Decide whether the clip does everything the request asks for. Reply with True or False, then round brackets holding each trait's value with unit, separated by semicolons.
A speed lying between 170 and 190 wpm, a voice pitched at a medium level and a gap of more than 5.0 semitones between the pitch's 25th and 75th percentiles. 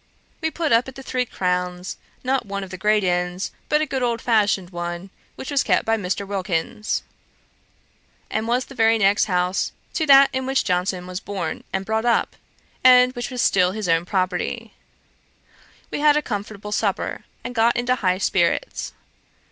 False (180 wpm; 210 Hz; 5.4 semitones)